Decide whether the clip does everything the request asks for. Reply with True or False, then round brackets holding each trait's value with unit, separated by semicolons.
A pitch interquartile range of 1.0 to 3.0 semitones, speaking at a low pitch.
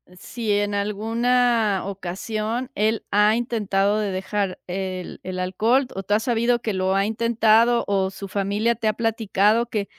False (2.7 semitones; 210 Hz)